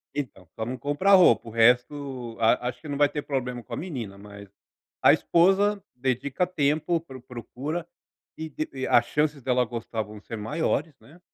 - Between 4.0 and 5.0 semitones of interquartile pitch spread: Yes, average, 4.6 semitones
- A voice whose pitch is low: Yes, low, 130 Hz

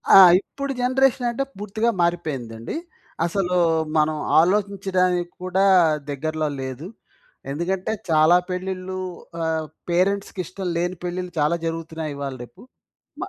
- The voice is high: No, medium, 180 Hz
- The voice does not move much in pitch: No, average, 3.5 semitones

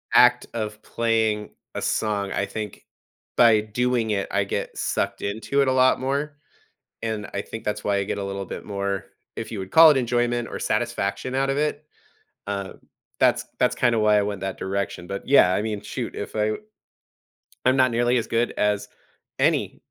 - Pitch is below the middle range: Yes, low, 110 Hz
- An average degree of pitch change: Yes, average, 3.5 semitones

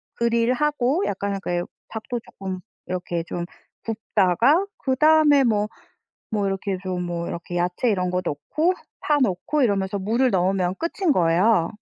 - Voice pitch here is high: Yes, high, 200 Hz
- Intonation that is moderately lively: No, wide, 5.8 semitones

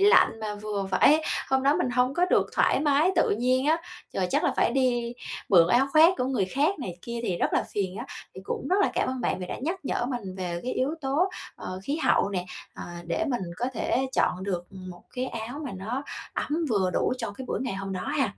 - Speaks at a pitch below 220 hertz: No, high, 245 Hz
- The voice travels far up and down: Yes, wide, 6.1 semitones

